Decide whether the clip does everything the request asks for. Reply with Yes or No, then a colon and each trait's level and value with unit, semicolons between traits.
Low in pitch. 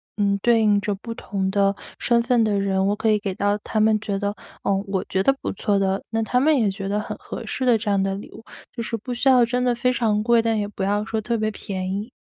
No: high, 210 Hz